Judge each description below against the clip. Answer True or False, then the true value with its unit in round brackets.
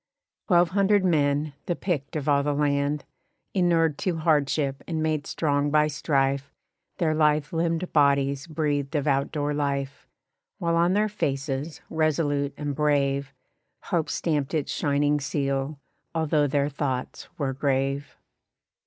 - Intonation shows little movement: True (2.2 semitones)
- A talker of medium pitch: True (145 Hz)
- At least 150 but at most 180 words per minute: False (135 wpm)